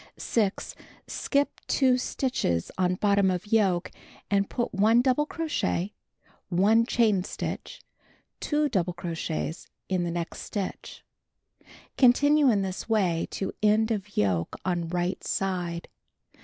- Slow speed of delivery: Yes, slow, 125 wpm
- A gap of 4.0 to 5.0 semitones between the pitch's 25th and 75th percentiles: Yes, average, 4.7 semitones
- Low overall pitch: No, high, 195 Hz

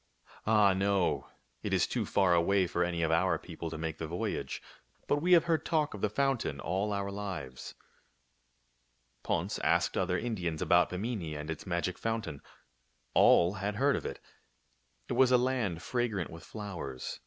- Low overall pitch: Yes, very low, 95 Hz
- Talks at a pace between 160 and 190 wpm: Yes, average, 175 wpm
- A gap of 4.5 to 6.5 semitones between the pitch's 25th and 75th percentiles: Yes, average, 4.9 semitones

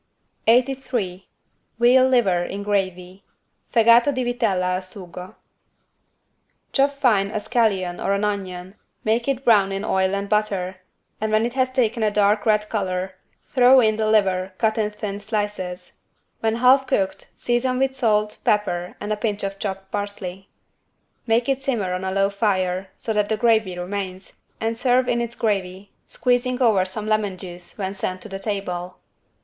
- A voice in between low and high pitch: No, high, 210 Hz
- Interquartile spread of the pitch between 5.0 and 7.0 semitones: No, average, 3.6 semitones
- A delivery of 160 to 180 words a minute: Yes, average, 165 wpm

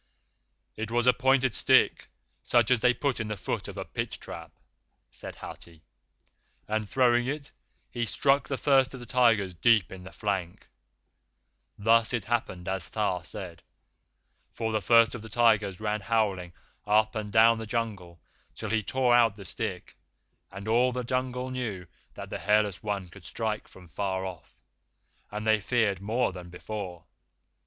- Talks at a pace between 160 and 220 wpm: Yes, average, 165 wpm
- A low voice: Yes, low, 110 Hz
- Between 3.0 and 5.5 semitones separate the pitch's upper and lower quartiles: Yes, average, 3.7 semitones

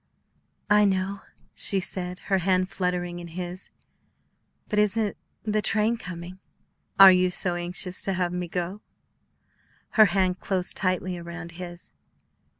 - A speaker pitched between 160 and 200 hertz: Yes, medium, 185 Hz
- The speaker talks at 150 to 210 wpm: No, slow, 135 wpm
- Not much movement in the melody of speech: Yes, narrow, 1.8 semitones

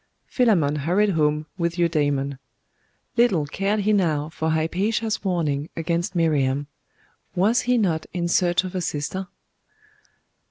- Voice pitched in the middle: Yes, medium, 170 Hz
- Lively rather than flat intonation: No, average, 4.4 semitones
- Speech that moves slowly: Yes, slow, 125 wpm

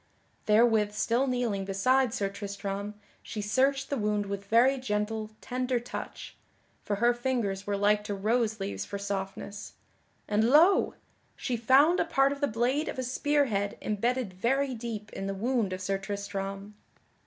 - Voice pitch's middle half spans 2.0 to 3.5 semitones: No, average, 4.1 semitones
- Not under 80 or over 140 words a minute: No, average, 165 wpm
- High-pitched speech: Yes, high, 215 Hz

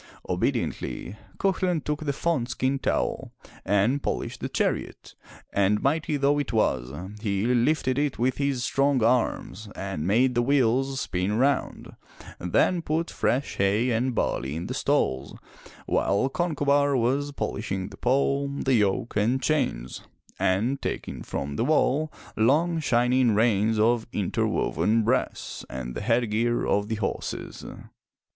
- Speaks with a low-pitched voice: Yes, low, 120 Hz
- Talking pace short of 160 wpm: Yes, average, 140 wpm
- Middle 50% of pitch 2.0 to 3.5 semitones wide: No, average, 5.1 semitones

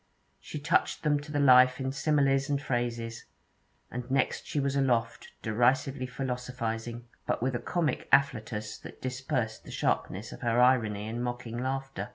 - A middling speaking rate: Yes, average, 160 wpm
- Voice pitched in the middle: No, low, 125 Hz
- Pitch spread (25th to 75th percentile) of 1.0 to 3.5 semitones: Yes, narrow, 2.6 semitones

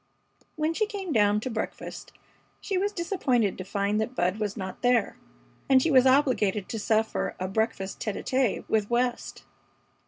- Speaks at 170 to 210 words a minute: Yes, average, 175 wpm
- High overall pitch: Yes, high, 225 Hz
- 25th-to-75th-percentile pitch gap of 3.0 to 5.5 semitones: Yes, average, 4.6 semitones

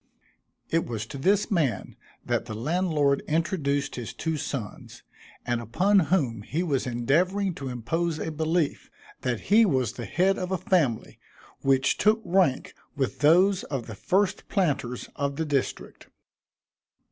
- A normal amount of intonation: No, wide, 6.1 semitones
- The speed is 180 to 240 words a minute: No, average, 145 wpm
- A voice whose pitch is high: No, medium, 150 Hz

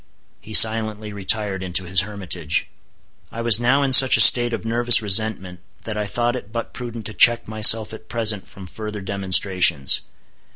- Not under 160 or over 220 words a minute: Yes, average, 170 wpm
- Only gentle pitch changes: No, average, 3.2 semitones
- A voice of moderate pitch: No, low, 110 Hz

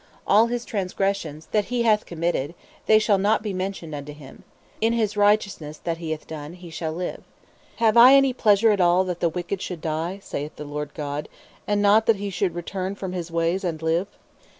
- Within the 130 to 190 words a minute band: No, fast, 205 wpm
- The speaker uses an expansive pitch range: No, average, 4.3 semitones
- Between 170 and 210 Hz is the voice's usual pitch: Yes, medium, 185 Hz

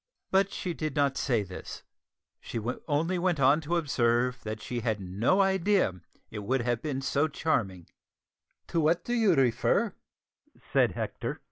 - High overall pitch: No, medium, 140 Hz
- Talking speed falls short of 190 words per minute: Yes, average, 145 wpm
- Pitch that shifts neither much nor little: No, wide, 6.4 semitones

